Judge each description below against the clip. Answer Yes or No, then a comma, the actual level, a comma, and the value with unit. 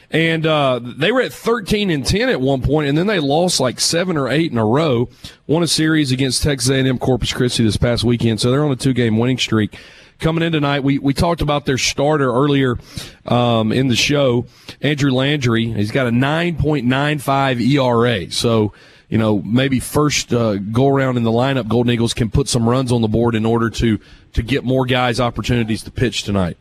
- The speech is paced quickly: Yes, fast, 215 wpm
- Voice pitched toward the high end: No, low, 130 Hz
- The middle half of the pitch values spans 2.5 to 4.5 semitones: Yes, average, 3.5 semitones